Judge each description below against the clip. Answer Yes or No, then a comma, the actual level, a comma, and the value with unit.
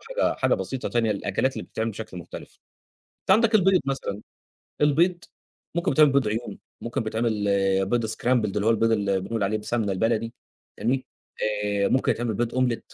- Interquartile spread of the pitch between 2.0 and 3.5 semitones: No, average, 3.9 semitones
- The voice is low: Yes, low, 115 Hz